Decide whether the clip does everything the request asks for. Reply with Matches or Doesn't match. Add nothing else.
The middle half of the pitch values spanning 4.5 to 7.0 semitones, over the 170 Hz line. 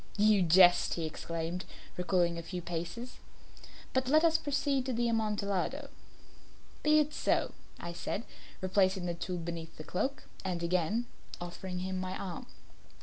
Matches